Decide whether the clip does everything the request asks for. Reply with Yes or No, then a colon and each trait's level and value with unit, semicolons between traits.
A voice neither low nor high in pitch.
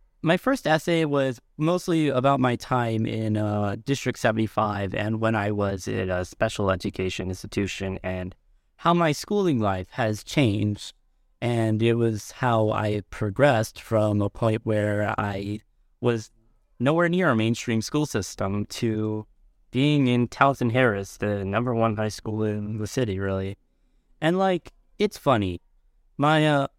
No: low, 110 Hz